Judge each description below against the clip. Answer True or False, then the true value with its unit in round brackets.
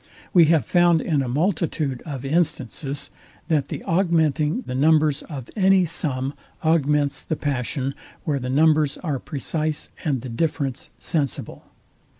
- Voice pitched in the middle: True (150 Hz)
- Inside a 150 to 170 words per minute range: False (140 wpm)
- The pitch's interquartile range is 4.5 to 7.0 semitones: False (2.9 semitones)